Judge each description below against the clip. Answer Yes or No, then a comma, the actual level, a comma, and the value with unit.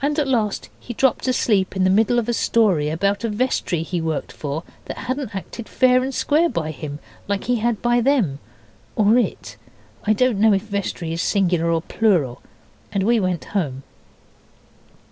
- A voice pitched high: Yes, high, 205 Hz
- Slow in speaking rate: No, average, 180 wpm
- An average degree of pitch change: No, wide, 5.8 semitones